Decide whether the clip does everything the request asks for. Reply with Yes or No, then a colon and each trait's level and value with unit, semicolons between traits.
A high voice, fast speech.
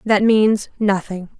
No: high, 205 Hz; slow, 130 wpm